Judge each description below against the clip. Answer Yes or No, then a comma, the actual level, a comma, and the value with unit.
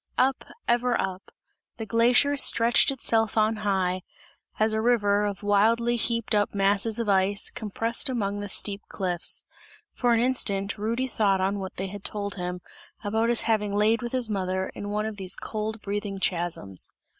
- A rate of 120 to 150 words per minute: No, average, 170 wpm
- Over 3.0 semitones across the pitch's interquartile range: No, average, 2.7 semitones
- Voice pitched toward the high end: Yes, high, 210 Hz